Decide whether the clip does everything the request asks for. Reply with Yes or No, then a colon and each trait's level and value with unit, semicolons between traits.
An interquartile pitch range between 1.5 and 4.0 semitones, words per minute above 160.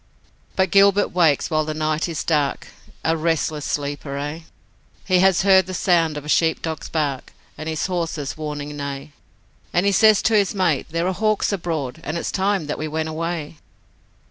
Yes: average, 3.7 semitones; average, 185 wpm